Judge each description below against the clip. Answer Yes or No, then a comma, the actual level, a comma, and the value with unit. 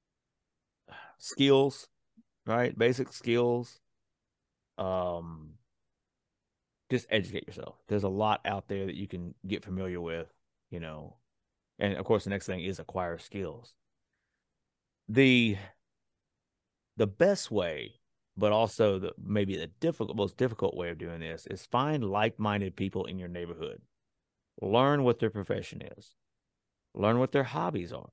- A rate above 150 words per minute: No, slow, 135 wpm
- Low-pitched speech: Yes, low, 100 Hz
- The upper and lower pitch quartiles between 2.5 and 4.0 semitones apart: No, average, 4.7 semitones